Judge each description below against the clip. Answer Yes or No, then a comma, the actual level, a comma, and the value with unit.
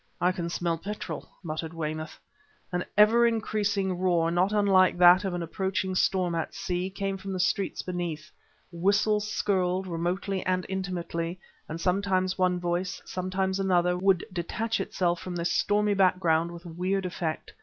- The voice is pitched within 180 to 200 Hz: Yes, medium, 185 Hz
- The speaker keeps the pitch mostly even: Yes, narrow, 2.0 semitones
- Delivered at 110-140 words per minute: No, average, 155 wpm